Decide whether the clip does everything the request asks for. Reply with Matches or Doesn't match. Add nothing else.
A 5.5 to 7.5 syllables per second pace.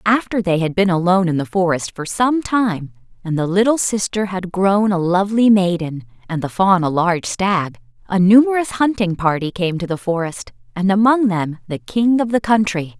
Doesn't match